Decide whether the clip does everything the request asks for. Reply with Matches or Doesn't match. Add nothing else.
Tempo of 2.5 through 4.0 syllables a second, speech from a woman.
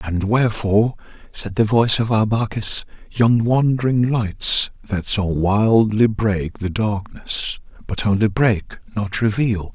Doesn't match